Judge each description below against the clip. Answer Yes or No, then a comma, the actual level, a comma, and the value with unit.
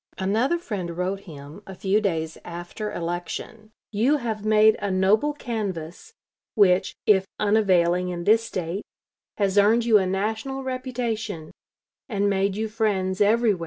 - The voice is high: Yes, high, 205 Hz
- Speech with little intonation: No, average, 3.2 semitones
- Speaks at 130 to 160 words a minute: Yes, average, 140 wpm